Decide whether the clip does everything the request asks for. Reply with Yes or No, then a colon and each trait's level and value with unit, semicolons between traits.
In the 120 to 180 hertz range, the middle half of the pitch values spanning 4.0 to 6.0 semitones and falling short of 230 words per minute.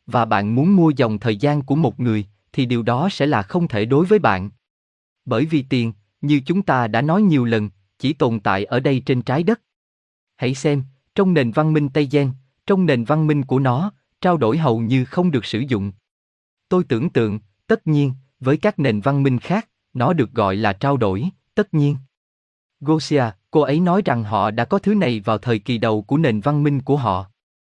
Yes: low, 135 Hz; wide, 5.4 semitones; average, 215 wpm